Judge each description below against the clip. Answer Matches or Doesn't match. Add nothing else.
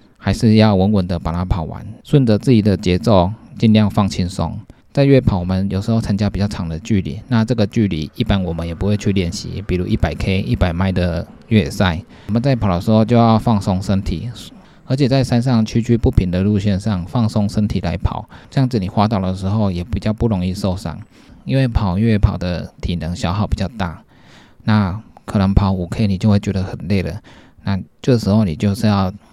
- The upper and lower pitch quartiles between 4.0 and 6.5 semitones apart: Doesn't match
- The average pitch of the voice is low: Matches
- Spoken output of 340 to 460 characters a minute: Doesn't match